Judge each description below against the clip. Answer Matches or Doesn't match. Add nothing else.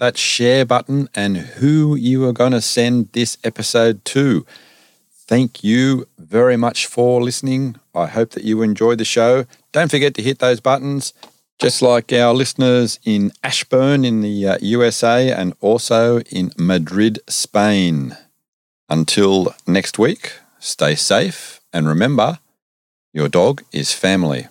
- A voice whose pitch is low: Matches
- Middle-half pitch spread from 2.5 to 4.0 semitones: Matches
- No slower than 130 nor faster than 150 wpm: Matches